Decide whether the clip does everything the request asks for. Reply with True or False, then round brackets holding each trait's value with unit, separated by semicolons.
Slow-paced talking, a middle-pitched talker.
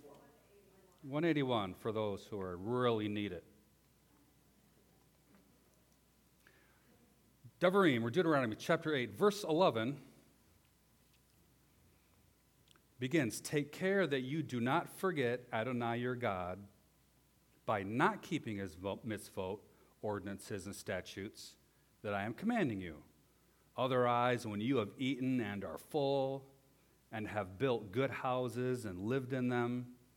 False (110 wpm; 125 Hz)